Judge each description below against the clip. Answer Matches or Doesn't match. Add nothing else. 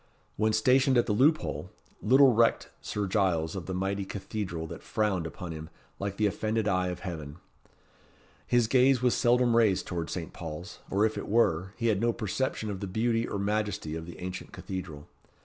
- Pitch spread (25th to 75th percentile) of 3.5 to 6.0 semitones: Matches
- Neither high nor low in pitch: Doesn't match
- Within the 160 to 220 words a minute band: Matches